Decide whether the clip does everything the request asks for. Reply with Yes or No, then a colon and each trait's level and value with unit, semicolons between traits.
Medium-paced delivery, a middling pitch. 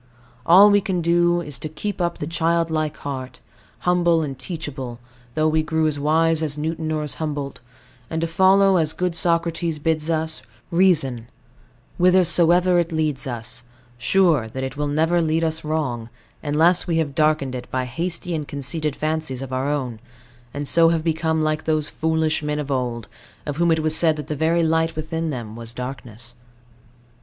Yes: average, 180 wpm; medium, 155 Hz